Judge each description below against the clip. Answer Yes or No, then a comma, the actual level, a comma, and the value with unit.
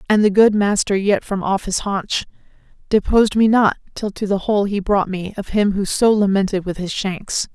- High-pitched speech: Yes, high, 200 Hz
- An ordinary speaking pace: No, fast, 215 wpm